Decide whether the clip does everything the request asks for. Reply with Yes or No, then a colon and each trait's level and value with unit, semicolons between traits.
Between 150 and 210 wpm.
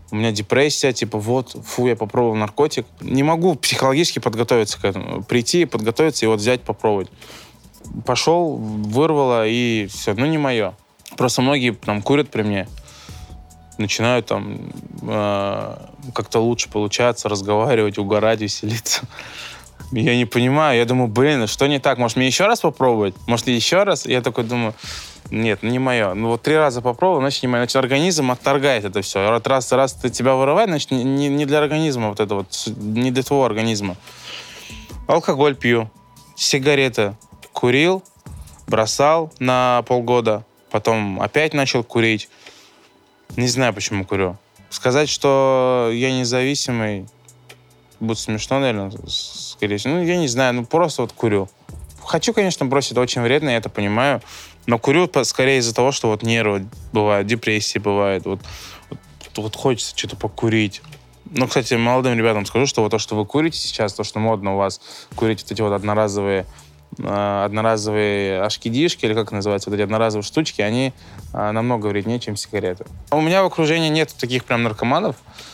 Yes: fast, 160 wpm